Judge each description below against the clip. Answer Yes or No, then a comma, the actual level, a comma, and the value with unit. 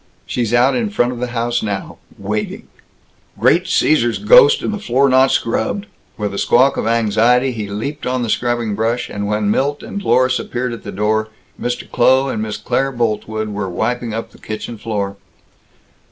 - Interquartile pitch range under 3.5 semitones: Yes, average, 3.0 semitones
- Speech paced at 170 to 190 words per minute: Yes, average, 180 wpm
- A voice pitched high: No, low, 120 Hz